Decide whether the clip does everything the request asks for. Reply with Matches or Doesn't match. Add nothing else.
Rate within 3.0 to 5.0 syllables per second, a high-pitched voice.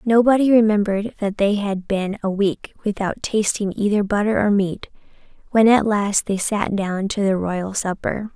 Matches